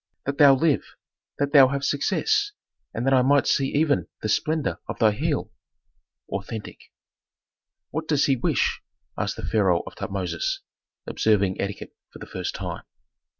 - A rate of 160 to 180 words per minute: No, average, 150 wpm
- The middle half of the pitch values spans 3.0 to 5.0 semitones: No, wide, 5.5 semitones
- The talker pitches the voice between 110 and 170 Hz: Yes, low, 135 Hz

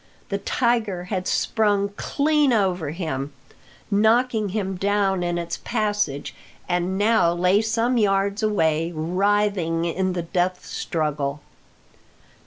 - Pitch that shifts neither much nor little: Yes, average, 3.6 semitones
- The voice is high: Yes, high, 195 Hz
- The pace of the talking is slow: Yes, slow, 115 wpm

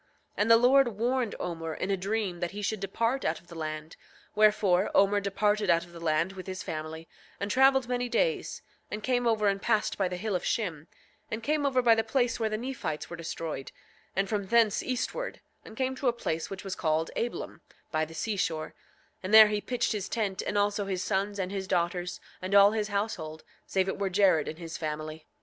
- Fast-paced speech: Yes, fast, 215 wpm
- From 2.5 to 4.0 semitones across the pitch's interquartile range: No, average, 4.4 semitones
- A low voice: No, high, 200 Hz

